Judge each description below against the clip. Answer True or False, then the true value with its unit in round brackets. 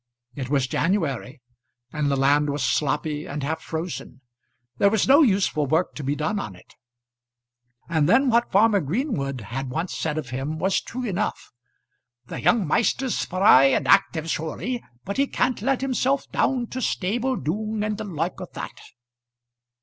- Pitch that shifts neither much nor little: False (7.2 semitones)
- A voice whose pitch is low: False (165 Hz)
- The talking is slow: False (165 wpm)